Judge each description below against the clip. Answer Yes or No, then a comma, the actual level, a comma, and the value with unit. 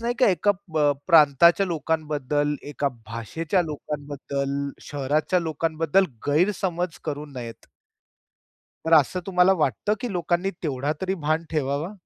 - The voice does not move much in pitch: No, average, 3.8 semitones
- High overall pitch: No, medium, 155 Hz